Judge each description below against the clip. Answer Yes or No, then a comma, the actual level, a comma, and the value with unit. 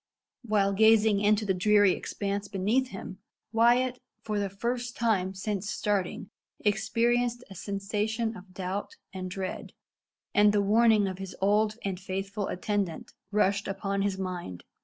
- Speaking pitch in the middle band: No, high, 205 Hz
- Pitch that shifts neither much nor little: No, narrow, 2.2 semitones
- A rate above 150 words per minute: No, average, 140 wpm